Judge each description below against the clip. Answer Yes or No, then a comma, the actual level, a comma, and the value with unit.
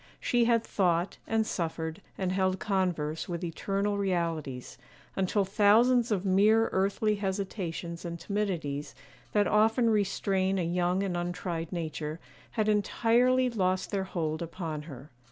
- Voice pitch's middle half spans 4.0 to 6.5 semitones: No, average, 3.6 semitones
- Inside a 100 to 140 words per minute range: Yes, slow, 135 wpm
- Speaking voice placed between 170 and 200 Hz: Yes, high, 190 Hz